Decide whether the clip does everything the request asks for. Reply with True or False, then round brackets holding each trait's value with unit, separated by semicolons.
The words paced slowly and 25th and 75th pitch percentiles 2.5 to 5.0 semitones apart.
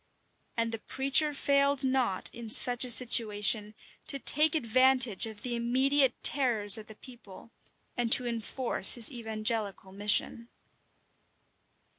True (125 wpm; 3.4 semitones)